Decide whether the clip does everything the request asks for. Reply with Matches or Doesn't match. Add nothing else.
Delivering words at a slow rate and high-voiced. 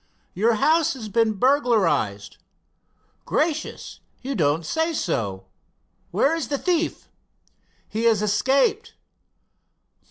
Matches